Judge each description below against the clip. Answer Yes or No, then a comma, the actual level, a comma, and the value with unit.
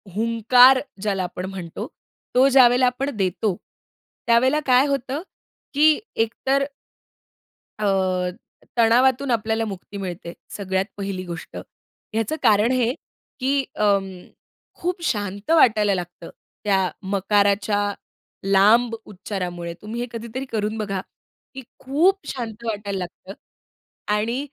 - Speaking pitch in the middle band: No, high, 215 Hz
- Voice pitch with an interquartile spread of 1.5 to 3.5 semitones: No, average, 4.4 semitones